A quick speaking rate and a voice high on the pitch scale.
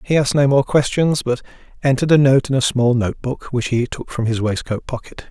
No: fast, 240 wpm; low, 130 Hz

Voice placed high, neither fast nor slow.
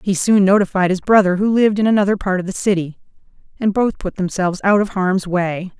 No: high, 195 Hz; fast, 215 wpm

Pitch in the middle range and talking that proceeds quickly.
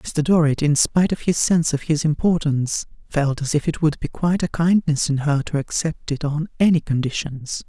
Yes: medium, 155 Hz; fast, 210 wpm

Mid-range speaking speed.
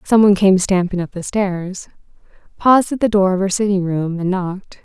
Yes: average, 185 wpm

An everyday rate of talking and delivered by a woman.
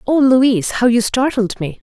Yes: average, 180 wpm; female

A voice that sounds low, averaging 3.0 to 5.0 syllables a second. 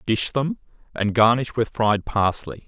Yes: low, 115 Hz; 4.1 syllables/s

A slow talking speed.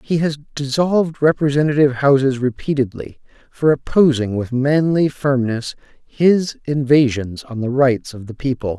Yes: slow, 130 wpm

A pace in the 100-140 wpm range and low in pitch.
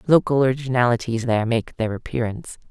Yes: slow, 135 wpm; low, 120 Hz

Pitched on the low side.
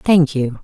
No: medium, 150 Hz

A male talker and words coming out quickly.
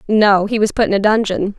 No: female; fast, 265 wpm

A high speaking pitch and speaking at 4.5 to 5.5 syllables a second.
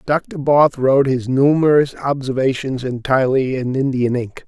No: low, 135 Hz; 4.7 syllables/s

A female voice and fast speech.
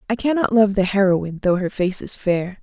Yes: female; fast, 230 wpm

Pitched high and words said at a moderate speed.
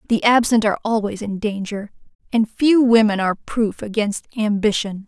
Yes: high, 215 Hz; average, 155 wpm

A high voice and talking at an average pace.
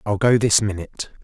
No: low, 105 Hz; average, 195 wpm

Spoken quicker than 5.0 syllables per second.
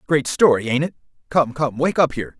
Yes: 5.8 syllables/s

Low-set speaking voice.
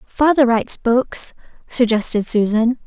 No: high, 240 Hz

